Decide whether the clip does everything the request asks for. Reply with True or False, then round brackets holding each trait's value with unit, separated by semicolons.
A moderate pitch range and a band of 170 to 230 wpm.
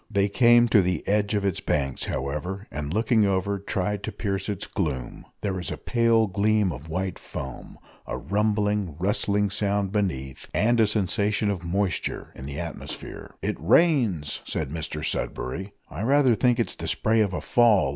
True (3.8 semitones; 175 wpm)